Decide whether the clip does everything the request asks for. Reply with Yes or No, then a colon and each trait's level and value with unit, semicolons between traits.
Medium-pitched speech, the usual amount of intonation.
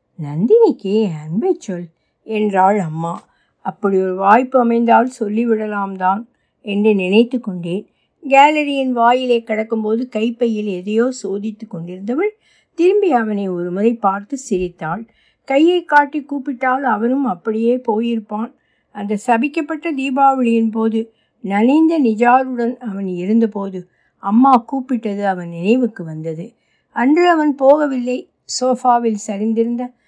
No: high, 230 Hz; average, 4.2 semitones